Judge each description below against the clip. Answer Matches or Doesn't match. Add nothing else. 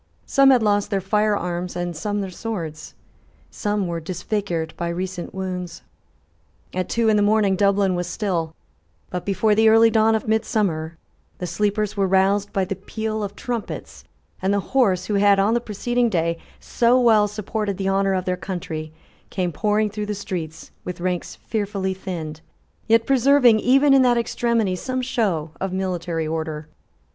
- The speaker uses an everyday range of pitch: Matches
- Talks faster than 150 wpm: Matches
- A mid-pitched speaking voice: Doesn't match